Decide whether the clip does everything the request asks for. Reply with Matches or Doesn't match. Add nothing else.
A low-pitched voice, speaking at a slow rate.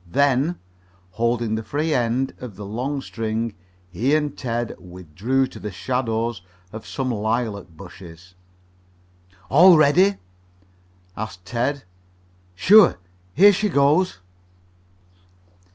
Matches